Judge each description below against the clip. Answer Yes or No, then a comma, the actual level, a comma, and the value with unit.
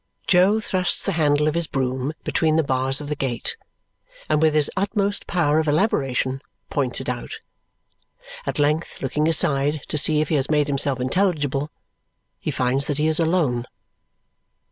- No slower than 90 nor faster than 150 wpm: No, average, 165 wpm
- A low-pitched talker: No, medium, 150 Hz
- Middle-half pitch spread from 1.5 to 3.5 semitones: Yes, average, 3.0 semitones